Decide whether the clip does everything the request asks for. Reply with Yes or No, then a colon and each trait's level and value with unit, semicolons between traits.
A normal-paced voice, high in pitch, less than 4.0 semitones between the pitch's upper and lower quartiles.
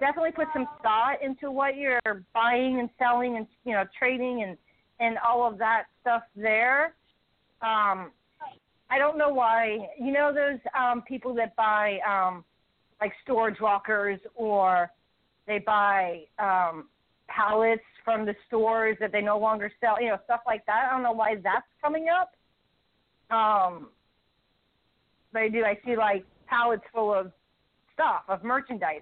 Yes: average, 155 wpm; high, 225 Hz; average, 3.3 semitones